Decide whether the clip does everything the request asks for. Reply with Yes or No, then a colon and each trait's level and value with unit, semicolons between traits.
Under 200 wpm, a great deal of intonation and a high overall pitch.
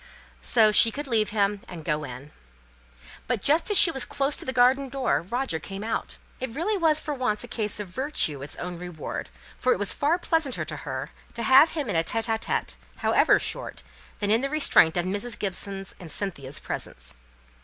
No: fast, 205 wpm; wide, 7.0 semitones; high, 220 Hz